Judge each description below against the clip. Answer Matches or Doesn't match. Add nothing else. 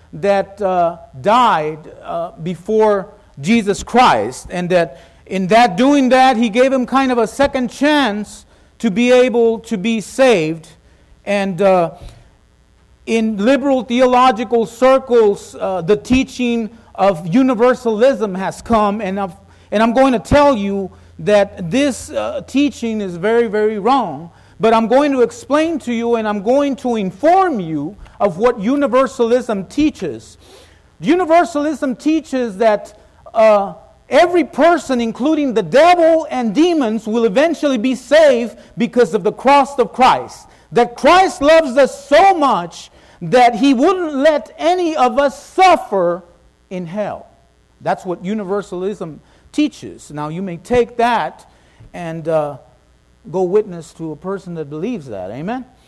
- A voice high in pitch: Matches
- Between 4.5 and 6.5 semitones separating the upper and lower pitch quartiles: Matches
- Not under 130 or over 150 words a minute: Matches